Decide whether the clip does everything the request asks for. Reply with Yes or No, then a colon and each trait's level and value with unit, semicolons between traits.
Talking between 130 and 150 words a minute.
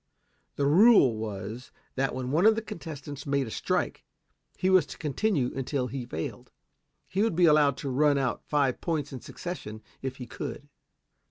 No: average, 175 wpm